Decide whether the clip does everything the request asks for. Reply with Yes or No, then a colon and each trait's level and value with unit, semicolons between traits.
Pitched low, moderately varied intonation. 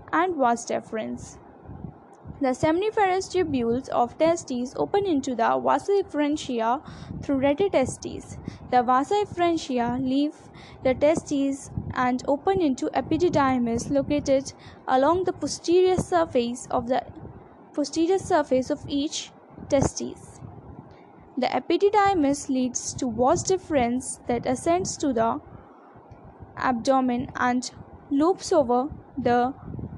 No: very high, 280 Hz; average, 4.7 semitones